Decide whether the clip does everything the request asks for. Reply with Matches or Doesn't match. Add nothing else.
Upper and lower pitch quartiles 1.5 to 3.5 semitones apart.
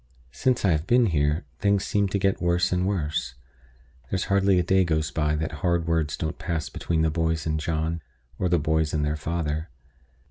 Matches